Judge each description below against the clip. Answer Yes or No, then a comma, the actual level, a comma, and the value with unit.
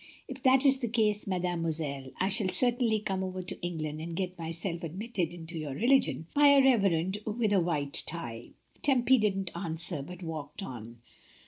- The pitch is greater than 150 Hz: Yes, medium, 185 Hz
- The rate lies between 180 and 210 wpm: Yes, average, 185 wpm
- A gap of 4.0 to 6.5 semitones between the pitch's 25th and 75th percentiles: Yes, average, 5.1 semitones